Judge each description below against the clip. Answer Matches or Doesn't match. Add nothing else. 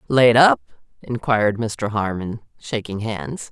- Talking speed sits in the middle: Doesn't match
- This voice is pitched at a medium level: Doesn't match